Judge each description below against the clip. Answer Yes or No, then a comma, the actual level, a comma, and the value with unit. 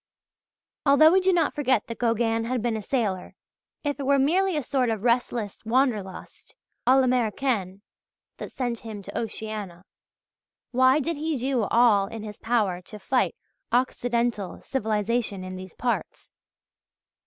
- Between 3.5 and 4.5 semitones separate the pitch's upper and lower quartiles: Yes, average, 4.0 semitones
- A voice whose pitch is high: Yes, high, 235 Hz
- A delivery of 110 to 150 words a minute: Yes, average, 145 wpm